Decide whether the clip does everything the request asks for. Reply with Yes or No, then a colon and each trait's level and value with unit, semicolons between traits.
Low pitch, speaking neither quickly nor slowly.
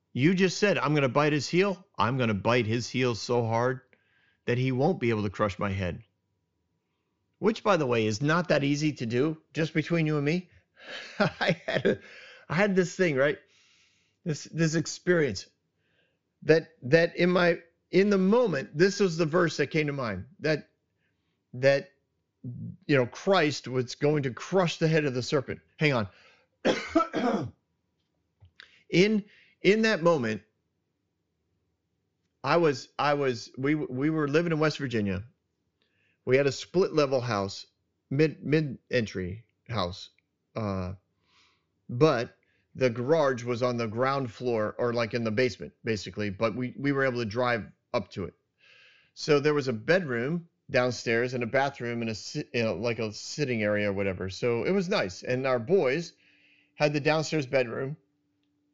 Yes: low, 130 Hz; average, 160 wpm